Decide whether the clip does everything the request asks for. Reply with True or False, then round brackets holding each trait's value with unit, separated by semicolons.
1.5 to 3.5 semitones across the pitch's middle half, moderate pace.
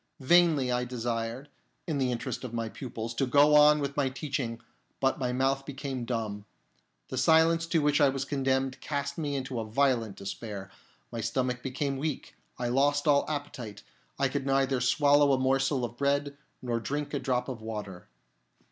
True (2.9 semitones; 175 wpm)